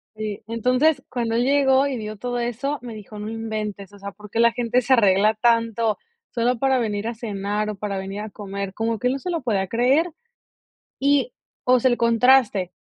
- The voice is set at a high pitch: Yes, high, 230 Hz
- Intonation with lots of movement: No, average, 3.2 semitones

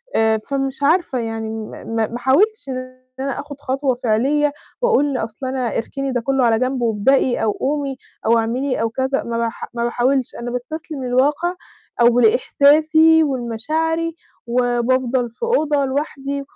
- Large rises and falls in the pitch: No, average, 3.3 semitones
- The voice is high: Yes, very high, 260 Hz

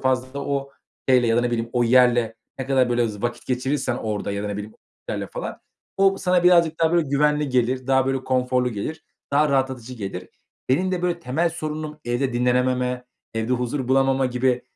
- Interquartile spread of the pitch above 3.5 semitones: No, average, 2.8 semitones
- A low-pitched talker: Yes, low, 130 Hz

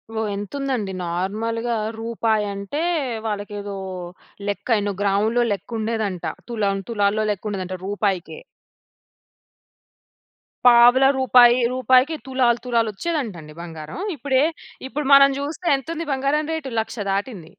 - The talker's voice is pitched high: Yes, high, 225 Hz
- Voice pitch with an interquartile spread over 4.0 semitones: Yes, average, 4.5 semitones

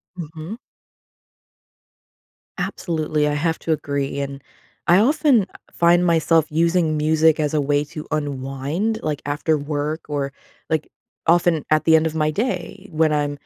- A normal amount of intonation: No, narrow, 2.3 semitones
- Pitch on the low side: No, medium, 155 Hz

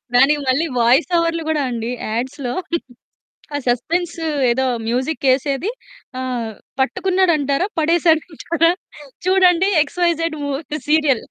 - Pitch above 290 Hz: Yes, very high, 305 Hz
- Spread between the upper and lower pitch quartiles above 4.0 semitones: Yes, average, 4.6 semitones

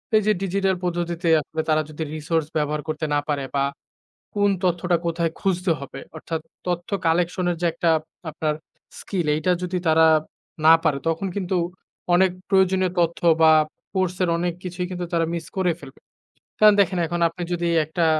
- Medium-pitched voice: Yes, medium, 175 Hz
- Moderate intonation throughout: No, narrow, 2.3 semitones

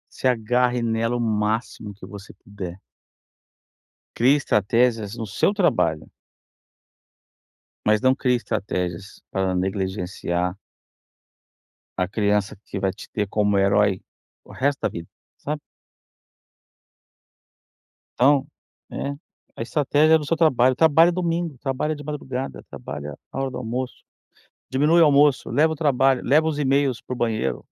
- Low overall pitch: Yes, low, 120 Hz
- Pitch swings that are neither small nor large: No, wide, 5.8 semitones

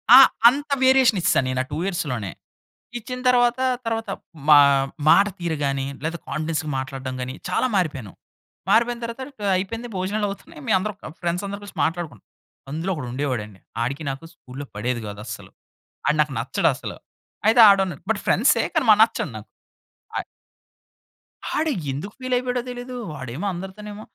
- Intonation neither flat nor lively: No, wide, 8.7 semitones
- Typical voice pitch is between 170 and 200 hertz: Yes, medium, 185 Hz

